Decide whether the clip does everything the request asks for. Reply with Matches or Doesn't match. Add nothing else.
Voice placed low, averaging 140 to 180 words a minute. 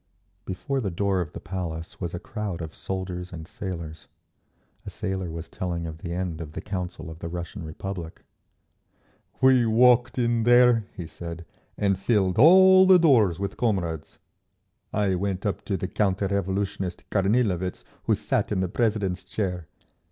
Matches